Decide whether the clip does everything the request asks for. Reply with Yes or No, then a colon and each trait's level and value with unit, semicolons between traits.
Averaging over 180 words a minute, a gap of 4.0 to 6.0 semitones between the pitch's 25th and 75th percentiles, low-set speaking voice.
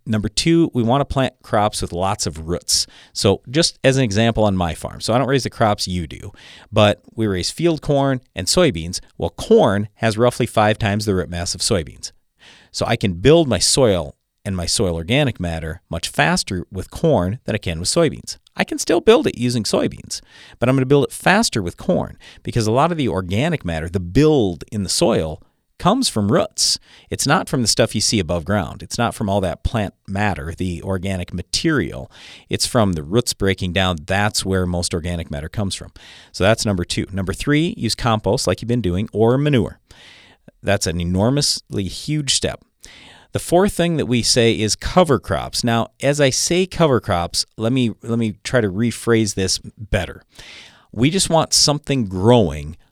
Yes: average, 200 wpm; wide, 5.4 semitones; low, 105 Hz